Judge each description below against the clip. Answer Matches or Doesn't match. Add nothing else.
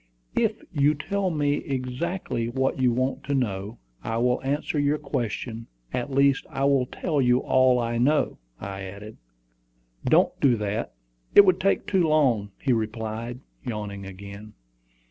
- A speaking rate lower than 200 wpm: Matches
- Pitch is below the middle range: Matches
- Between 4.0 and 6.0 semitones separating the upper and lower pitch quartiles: Matches